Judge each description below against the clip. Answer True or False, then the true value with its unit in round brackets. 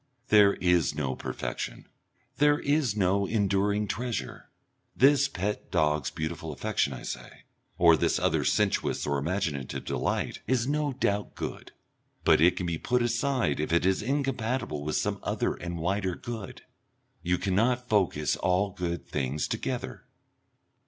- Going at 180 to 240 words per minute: False (145 wpm)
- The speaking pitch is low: True (95 Hz)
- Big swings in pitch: True (6.6 semitones)